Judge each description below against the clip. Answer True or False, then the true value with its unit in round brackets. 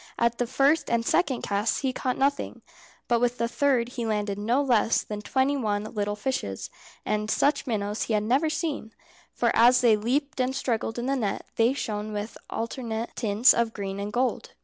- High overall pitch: True (235 Hz)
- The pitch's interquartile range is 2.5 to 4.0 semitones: True (3.7 semitones)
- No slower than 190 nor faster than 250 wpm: True (195 wpm)